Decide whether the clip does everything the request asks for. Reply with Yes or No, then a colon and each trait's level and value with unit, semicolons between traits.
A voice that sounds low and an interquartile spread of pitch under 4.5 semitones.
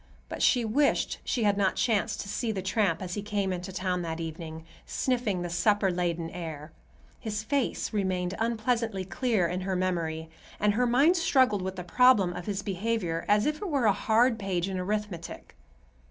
No: high, 195 Hz; average, 4.0 semitones